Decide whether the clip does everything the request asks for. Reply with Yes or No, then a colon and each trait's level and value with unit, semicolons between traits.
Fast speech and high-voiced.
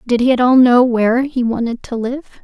Yes: fast, 245 wpm; high, 245 Hz